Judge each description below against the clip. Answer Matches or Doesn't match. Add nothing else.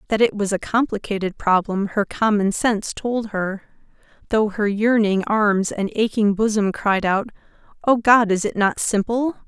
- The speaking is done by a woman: Matches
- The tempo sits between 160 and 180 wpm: Matches